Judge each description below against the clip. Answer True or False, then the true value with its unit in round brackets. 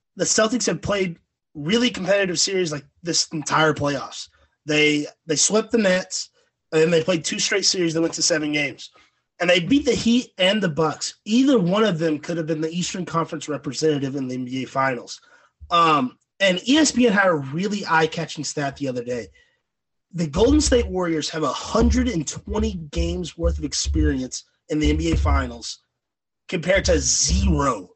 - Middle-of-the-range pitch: True (165 Hz)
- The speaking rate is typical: True (175 wpm)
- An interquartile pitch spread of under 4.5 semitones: False (5.6 semitones)